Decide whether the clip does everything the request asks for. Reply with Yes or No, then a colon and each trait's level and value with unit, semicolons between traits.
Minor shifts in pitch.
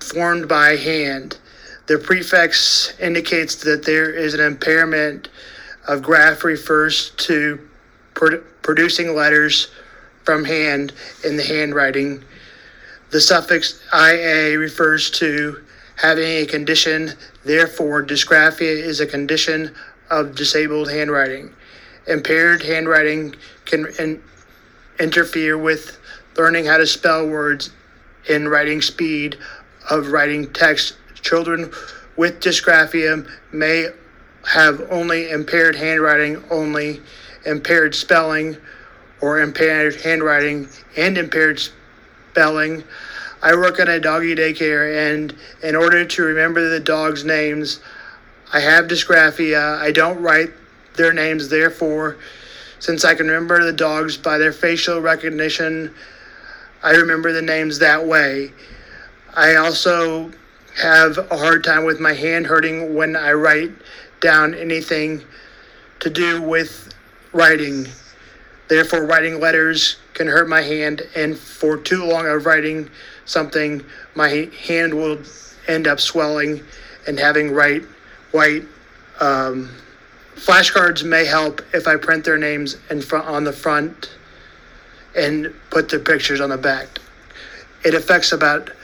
Yes: narrow, 1.4 semitones